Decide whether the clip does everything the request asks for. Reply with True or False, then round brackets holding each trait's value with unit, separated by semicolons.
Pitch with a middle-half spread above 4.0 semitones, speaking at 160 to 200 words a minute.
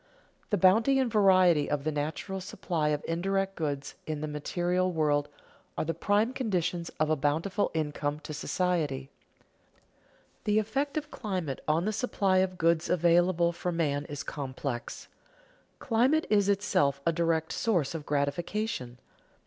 False (4.7 semitones; 145 wpm)